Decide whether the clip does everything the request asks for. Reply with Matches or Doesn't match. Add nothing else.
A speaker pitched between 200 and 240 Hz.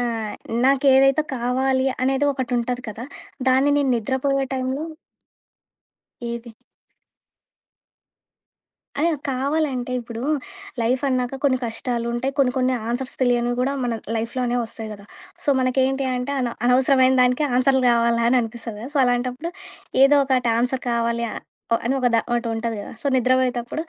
Doesn't match